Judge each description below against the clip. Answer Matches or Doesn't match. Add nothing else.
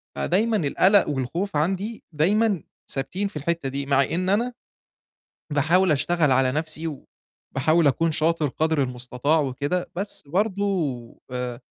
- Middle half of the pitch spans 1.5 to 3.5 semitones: Doesn't match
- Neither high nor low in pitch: Matches